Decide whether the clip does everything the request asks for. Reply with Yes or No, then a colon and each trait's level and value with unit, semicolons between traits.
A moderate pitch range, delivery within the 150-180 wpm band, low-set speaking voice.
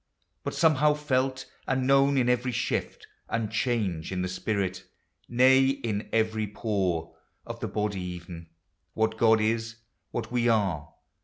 Yes: average, 5.0 semitones; average, 155 wpm; low, 110 Hz